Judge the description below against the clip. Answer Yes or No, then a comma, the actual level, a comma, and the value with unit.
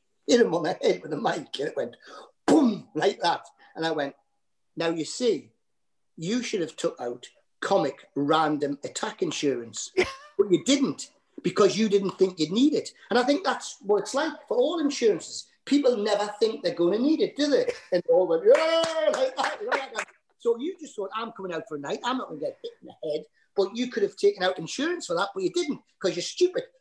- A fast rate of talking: Yes, fast, 230 wpm